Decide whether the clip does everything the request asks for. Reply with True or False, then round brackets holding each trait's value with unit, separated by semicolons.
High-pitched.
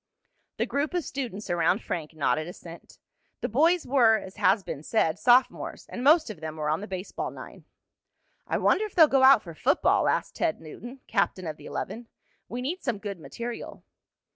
True (220 Hz)